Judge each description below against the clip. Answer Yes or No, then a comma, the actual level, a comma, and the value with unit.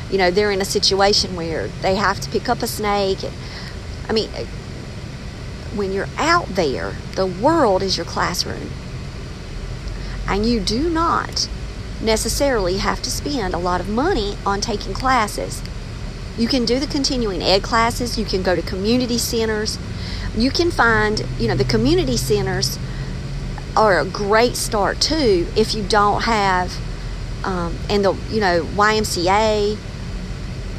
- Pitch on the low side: No, high, 205 Hz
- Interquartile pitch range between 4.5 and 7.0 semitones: No, average, 3.9 semitones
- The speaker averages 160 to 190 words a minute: No, average, 150 wpm